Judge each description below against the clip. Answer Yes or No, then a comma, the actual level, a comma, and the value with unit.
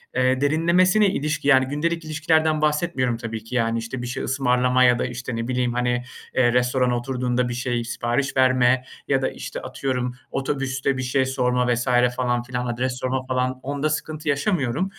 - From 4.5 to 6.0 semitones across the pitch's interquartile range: No, narrow, 2.6 semitones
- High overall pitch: No, low, 130 Hz